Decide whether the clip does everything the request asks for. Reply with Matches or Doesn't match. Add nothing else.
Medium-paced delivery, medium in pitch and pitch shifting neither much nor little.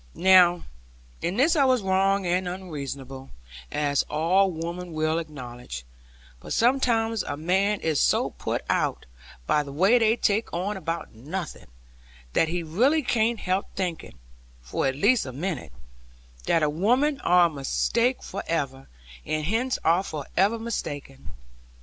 Doesn't match